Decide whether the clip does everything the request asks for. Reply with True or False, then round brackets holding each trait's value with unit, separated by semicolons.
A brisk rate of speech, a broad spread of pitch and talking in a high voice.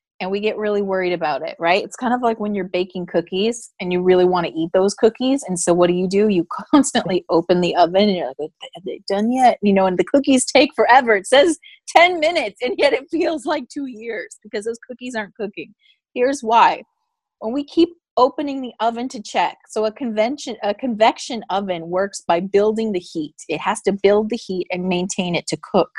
True (225 wpm; 5.7 semitones; 215 Hz)